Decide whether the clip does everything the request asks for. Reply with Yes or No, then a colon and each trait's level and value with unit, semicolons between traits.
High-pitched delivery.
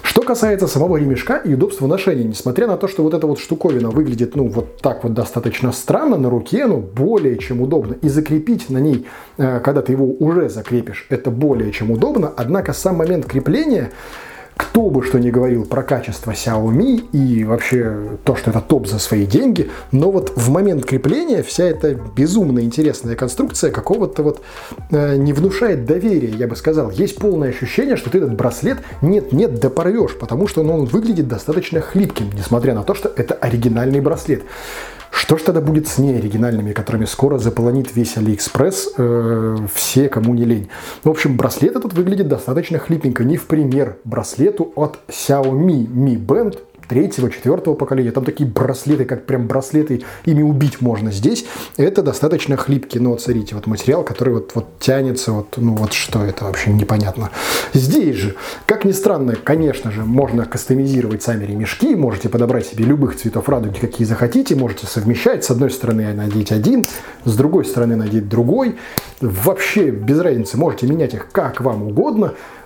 No: low, 130 Hz